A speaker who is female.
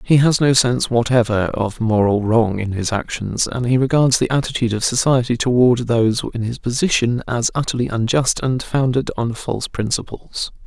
No: male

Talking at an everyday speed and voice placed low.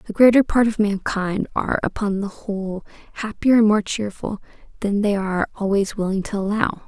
No: average, 175 wpm; high, 205 Hz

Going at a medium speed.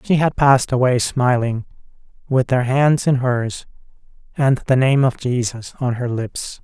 Yes: average, 165 wpm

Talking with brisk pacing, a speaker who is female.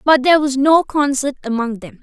Yes: fast, 210 wpm; female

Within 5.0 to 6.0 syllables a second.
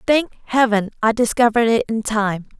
Yes: 5.2 syllables/s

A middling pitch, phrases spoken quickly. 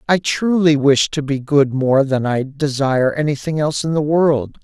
No: medium, 145 Hz; average, 195 wpm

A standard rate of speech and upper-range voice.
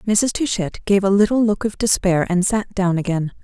No: fast, 210 wpm; high, 195 Hz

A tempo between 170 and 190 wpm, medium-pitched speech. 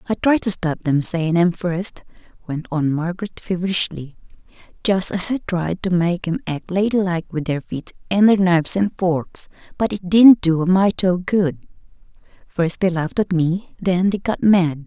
Yes: average, 185 wpm; medium, 180 Hz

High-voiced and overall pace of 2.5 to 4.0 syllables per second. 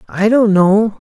Yes: high, 205 Hz; 3.6 syllables/s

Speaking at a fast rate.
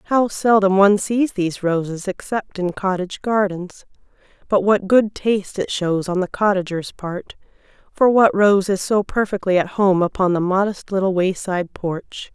No: average, 165 wpm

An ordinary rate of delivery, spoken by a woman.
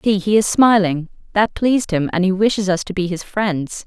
No: fast, 235 wpm; female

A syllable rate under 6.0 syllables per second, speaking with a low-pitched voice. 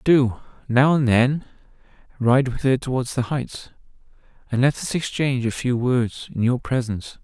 Yes: 4.8 syllables/s; low, 125 Hz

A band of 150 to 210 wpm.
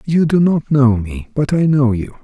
No: fast, 240 wpm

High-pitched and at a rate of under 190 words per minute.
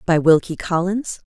No: medium, 175 Hz; slow, 135 wpm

